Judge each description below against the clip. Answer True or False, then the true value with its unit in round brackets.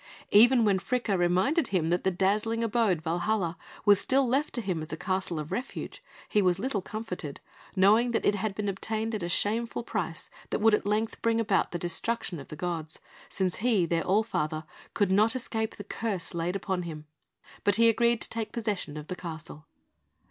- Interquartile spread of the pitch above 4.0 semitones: True (4.4 semitones)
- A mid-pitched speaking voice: False (200 Hz)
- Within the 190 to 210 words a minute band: True (200 wpm)